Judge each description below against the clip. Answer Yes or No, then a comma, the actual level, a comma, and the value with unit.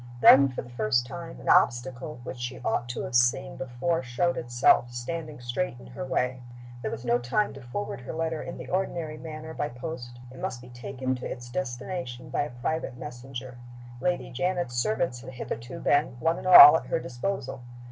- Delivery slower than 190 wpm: No, average, 195 wpm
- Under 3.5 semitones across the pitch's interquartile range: No, average, 4.1 semitones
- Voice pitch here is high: No, low, 130 Hz